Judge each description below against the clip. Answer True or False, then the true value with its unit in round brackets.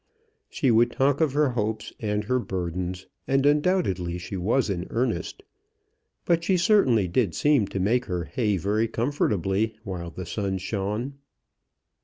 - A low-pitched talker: True (110 Hz)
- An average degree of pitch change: False (6.1 semitones)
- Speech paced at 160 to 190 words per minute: False (150 wpm)